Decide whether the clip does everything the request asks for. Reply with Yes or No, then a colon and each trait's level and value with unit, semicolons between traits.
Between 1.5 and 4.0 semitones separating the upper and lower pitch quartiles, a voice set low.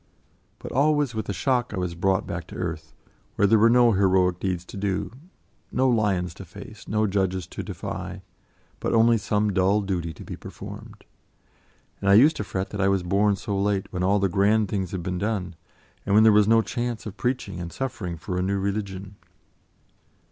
Yes: average, 2.7 semitones; low, 100 Hz